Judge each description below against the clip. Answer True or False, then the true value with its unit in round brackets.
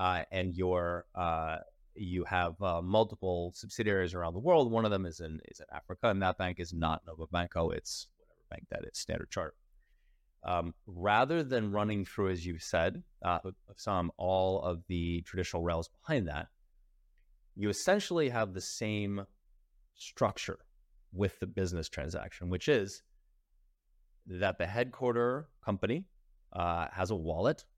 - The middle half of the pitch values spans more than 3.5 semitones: False (3.2 semitones)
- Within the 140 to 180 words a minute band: True (155 wpm)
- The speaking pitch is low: True (90 Hz)